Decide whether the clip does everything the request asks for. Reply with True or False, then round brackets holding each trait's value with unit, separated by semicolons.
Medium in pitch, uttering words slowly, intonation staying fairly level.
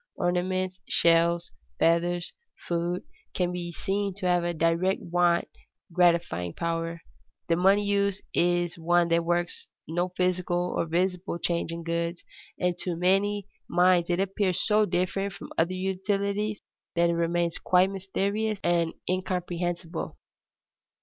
True (175 Hz; 130 wpm; 1.8 semitones)